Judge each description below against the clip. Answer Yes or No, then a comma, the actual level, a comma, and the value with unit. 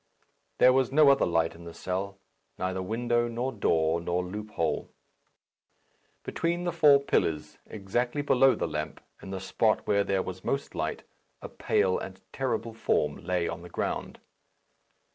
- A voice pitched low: Yes, low, 100 Hz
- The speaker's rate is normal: Yes, average, 155 wpm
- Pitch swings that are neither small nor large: No, wide, 6.1 semitones